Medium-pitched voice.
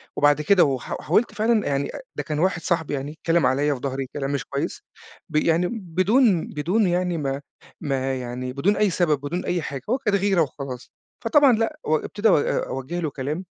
Yes: medium, 160 Hz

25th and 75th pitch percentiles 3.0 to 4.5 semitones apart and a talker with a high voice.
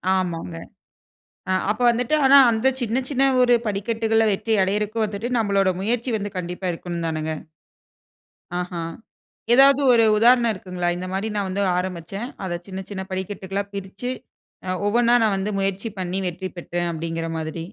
Yes: average, 4.0 semitones; high, 195 Hz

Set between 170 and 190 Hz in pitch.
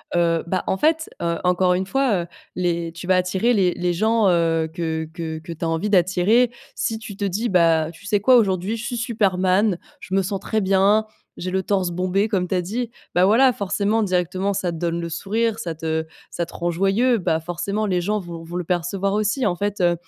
Yes: medium, 185 Hz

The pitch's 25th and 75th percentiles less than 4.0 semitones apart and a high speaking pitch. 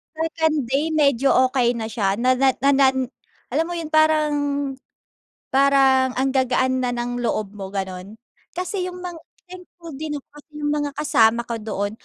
No: average, 4.5 semitones; very high, 270 Hz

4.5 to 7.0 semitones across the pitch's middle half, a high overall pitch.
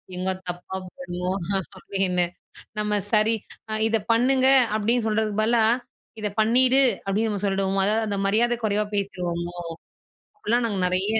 No: average, 2.9 semitones; high, 210 Hz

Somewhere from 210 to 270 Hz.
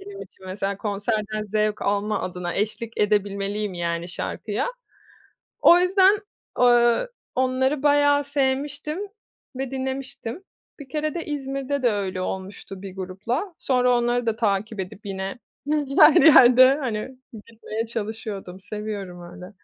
Yes: high, 225 Hz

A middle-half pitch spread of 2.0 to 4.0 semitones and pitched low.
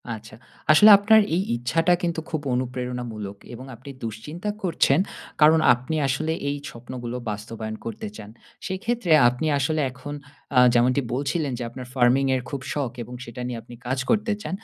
No: average, 4.8 semitones; low, 130 Hz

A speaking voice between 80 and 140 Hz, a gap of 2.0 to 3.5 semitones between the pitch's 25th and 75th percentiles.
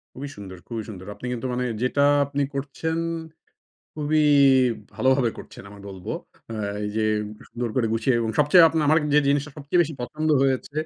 No: low, 135 Hz; average, 4.4 semitones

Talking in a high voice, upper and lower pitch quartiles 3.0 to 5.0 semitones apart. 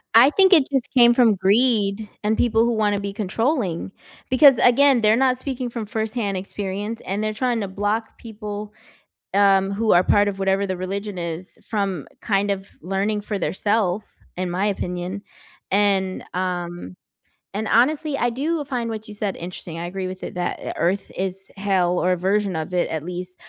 Yes: high, 205 Hz; average, 3.4 semitones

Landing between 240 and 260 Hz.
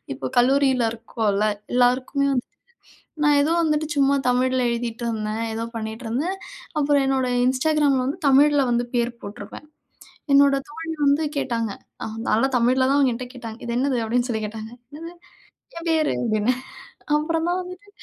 Yes: very high, 255 Hz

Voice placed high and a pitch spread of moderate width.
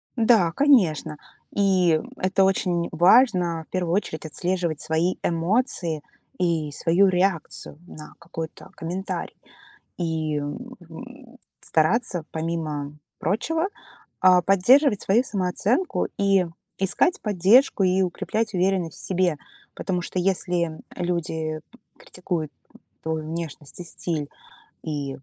No: medium, 180 Hz; average, 3.4 semitones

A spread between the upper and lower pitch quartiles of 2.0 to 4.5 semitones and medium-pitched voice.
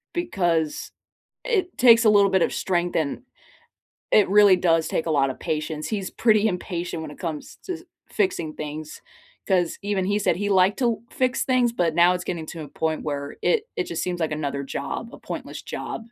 No: average, 5.2 semitones; medium, 180 Hz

